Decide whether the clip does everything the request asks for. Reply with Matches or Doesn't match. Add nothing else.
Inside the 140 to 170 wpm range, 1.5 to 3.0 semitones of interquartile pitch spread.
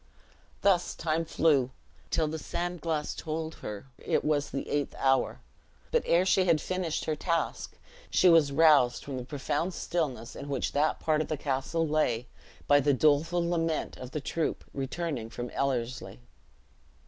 Doesn't match